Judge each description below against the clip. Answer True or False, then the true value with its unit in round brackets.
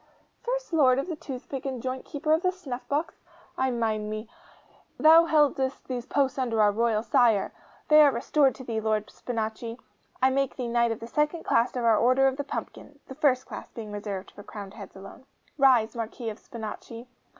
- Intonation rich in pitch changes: False (3.8 semitones)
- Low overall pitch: False (250 Hz)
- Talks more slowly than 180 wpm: False (195 wpm)